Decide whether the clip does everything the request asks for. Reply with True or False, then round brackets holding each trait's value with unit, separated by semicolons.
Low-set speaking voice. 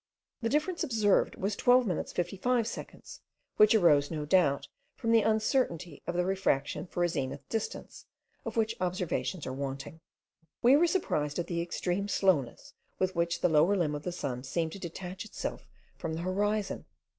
False (180 Hz)